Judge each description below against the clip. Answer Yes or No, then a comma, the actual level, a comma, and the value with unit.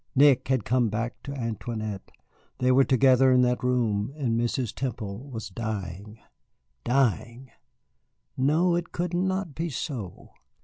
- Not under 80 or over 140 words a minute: Yes, slow, 135 wpm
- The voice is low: Yes, low, 125 Hz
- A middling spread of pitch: Yes, average, 3.5 semitones